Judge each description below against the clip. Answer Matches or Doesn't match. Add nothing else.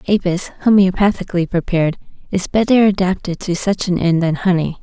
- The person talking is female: Matches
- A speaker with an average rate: Matches